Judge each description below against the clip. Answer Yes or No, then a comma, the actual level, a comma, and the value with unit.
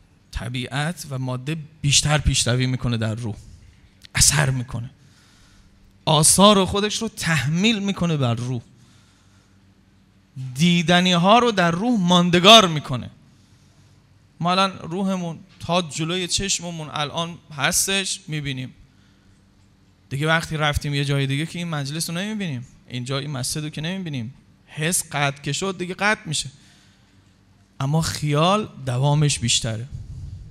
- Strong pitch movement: Yes, wide, 7.0 semitones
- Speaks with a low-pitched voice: No, medium, 145 Hz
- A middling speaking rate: Yes, average, 120 wpm